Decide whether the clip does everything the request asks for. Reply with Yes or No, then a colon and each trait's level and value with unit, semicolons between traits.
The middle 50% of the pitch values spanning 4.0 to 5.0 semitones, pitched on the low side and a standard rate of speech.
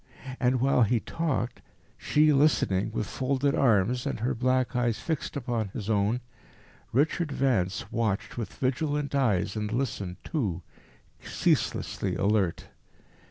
No: average, 4.7 semitones; low, 120 Hz; slow, 125 wpm